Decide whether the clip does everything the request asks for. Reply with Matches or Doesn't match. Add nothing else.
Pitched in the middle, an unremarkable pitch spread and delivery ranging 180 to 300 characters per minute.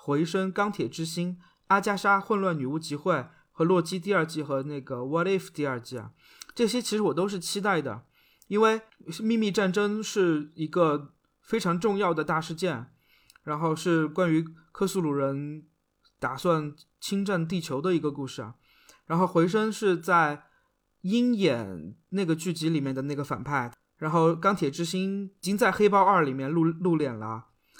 Matches